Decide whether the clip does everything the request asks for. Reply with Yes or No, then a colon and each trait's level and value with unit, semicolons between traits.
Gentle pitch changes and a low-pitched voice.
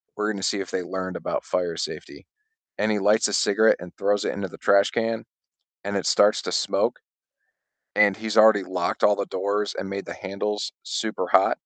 Yes: narrow, 1.6 semitones; low, 100 Hz